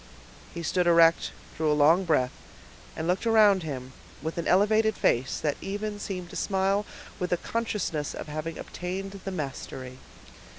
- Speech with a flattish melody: No, average, 4.2 semitones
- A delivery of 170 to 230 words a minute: No, average, 160 wpm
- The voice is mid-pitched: Yes, medium, 175 Hz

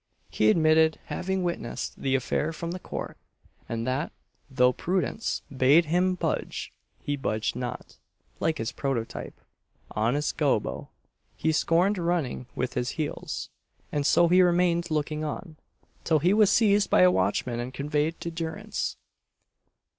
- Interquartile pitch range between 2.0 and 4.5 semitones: No, average, 5.2 semitones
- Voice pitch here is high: No, medium, 155 Hz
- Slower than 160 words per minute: Yes, average, 140 wpm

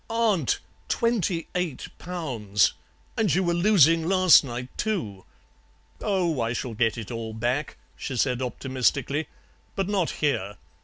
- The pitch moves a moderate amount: No, wide, 7.4 semitones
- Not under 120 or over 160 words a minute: Yes, slow, 135 wpm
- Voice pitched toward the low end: No, medium, 150 Hz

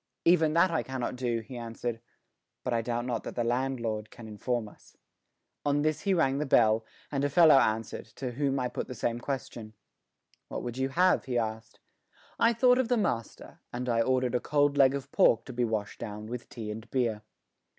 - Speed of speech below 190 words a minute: No, fast, 205 wpm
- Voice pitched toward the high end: No, low, 125 Hz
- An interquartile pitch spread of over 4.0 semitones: No, average, 3.5 semitones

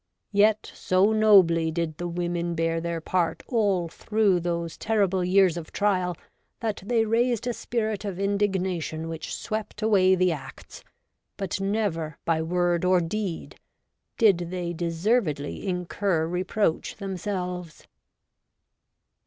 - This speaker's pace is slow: Yes, slow, 130 wpm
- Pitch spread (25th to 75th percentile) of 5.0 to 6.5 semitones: No, average, 3.4 semitones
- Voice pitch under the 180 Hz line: No, medium, 185 Hz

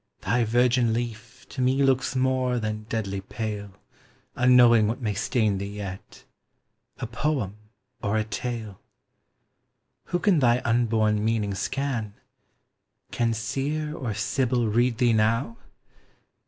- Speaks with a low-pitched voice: Yes, low, 115 Hz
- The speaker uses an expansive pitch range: No, average, 2.9 semitones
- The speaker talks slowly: Yes, slow, 125 wpm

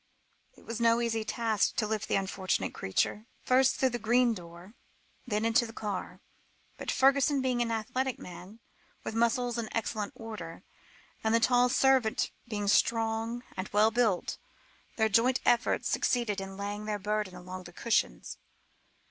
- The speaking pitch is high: Yes, high, 225 Hz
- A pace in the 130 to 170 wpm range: Yes, average, 160 wpm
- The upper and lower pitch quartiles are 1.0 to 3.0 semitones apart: Yes, average, 2.7 semitones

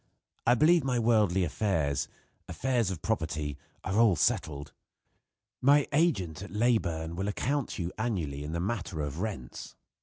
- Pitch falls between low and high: No, very low, 95 Hz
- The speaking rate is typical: Yes, average, 150 wpm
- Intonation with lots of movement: Yes, wide, 6.9 semitones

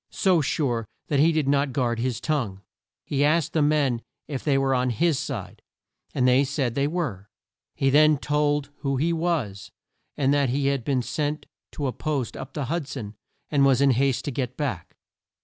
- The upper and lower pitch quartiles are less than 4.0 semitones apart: Yes, average, 2.8 semitones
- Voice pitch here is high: No, medium, 140 Hz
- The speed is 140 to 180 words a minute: No, average, 195 wpm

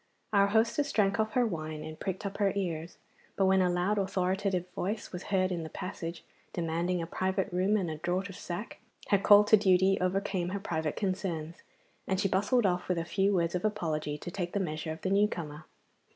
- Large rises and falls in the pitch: No, average, 2.7 semitones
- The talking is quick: Yes, fast, 210 wpm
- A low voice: No, medium, 185 Hz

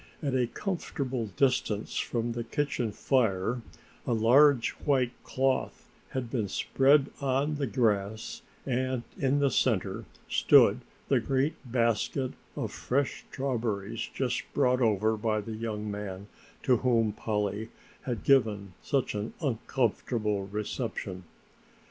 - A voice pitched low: Yes, low, 120 Hz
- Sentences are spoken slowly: Yes, slow, 125 wpm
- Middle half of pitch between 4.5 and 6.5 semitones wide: No, average, 3.7 semitones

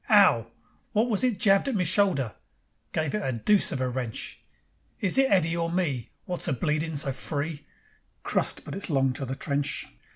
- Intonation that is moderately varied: No, wide, 6.5 semitones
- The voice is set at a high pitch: No, medium, 160 Hz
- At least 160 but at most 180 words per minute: No, average, 190 wpm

